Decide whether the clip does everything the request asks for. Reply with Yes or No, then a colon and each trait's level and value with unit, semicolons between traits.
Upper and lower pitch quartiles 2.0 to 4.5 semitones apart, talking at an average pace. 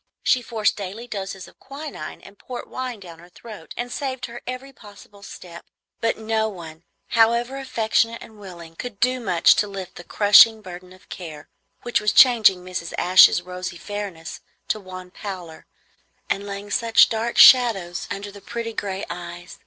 Yes: average, 4.2 semitones; average, 170 wpm